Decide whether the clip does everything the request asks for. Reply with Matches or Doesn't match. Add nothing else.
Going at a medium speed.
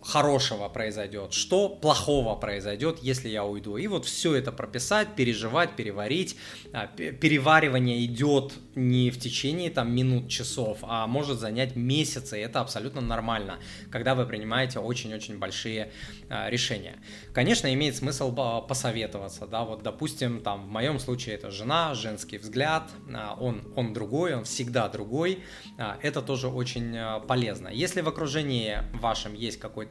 Matches